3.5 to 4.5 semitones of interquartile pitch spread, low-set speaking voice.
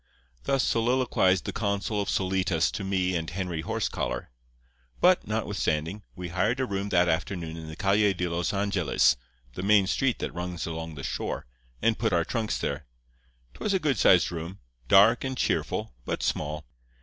Yes: average, 3.9 semitones; very low, 95 Hz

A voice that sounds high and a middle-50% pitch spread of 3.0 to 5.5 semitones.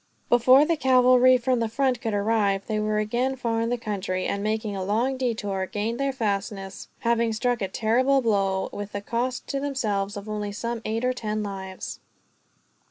Yes: high, 225 Hz; average, 3.5 semitones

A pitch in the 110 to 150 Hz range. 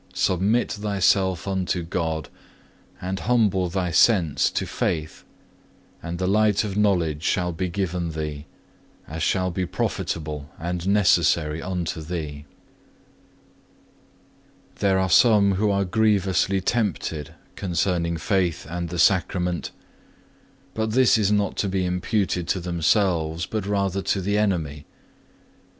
No: very low, 90 Hz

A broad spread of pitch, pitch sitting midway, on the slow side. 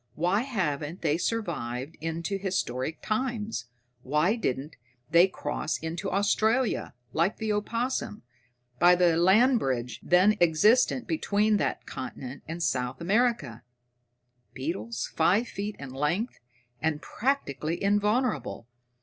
Yes: wide, 6.3 semitones; medium, 175 Hz; slow, 115 wpm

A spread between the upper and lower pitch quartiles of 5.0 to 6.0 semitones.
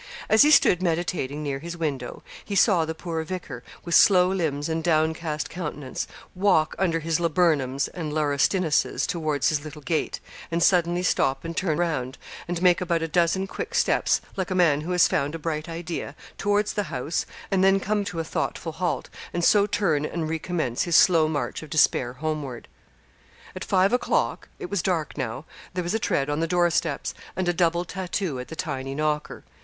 No: average, 3.1 semitones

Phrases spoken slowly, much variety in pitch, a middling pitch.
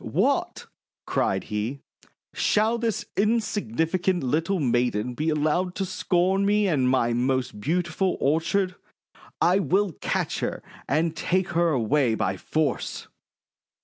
Yes: slow, 120 wpm; wide, 6.4 semitones; medium, 165 Hz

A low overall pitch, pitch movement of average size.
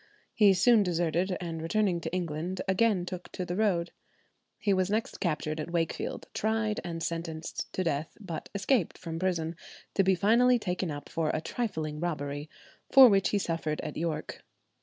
No: medium, 175 Hz; average, 3.5 semitones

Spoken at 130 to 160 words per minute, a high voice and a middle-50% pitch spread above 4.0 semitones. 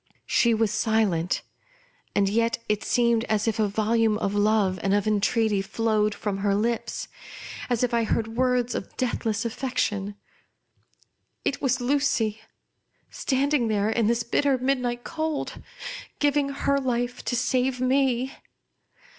No: average, 145 wpm; high, 230 Hz; average, 3.1 semitones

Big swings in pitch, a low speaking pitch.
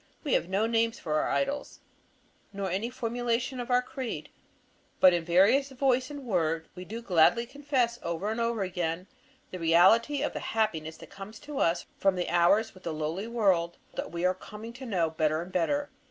No: wide, 5.8 semitones; high, 205 Hz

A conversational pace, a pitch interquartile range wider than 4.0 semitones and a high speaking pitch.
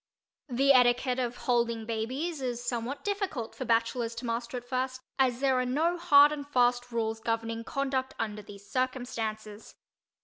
No: average, 160 wpm; narrow, 2.4 semitones; high, 245 Hz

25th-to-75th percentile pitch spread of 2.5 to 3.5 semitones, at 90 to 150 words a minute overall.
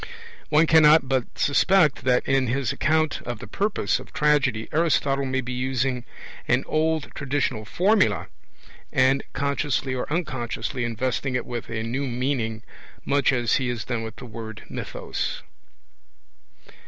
Yes: average, 3.1 semitones; average, 145 wpm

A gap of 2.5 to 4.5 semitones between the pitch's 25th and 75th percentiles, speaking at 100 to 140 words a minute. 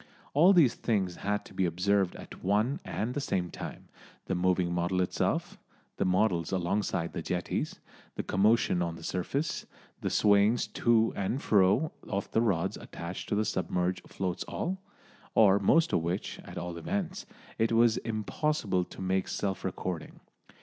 No: average, 4.0 semitones; average, 160 wpm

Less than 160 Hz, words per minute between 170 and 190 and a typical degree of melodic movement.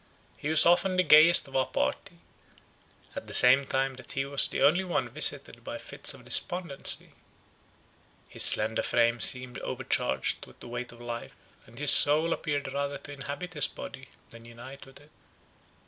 Yes: medium, 140 Hz; average, 175 wpm; average, 3.6 semitones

